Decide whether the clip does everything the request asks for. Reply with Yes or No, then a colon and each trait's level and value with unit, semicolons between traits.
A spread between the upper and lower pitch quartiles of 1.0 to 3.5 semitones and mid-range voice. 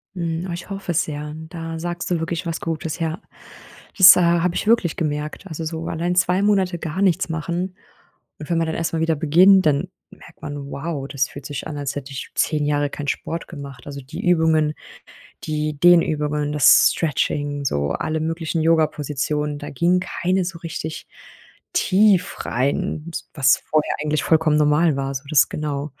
Yes: average, 2.7 semitones; medium, 160 Hz